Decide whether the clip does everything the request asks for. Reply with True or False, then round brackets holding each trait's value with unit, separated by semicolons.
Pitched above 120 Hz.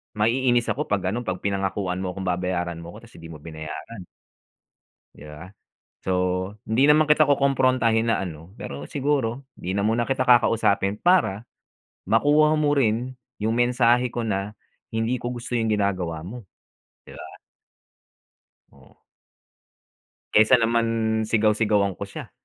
False (110 Hz)